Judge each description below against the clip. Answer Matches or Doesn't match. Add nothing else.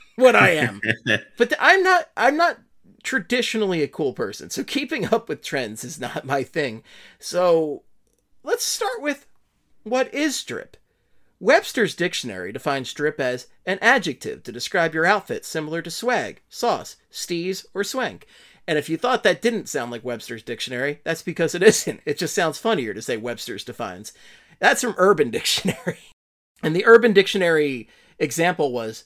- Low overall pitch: Doesn't match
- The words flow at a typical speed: Matches